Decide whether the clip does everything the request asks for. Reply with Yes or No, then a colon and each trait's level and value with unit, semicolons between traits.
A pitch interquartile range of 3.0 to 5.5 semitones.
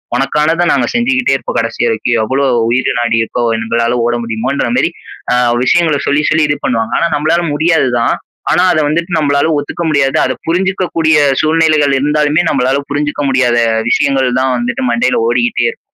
Yes: average, 4.2 semitones